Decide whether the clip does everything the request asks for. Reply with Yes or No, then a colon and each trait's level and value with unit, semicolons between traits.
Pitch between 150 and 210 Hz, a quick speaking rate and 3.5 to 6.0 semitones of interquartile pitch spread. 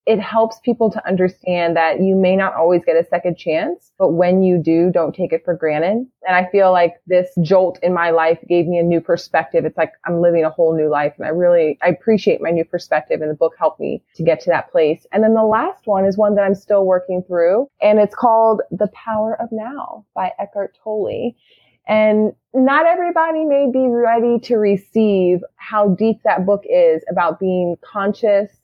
Yes: high, 190 Hz; fast, 210 wpm; average, 4.3 semitones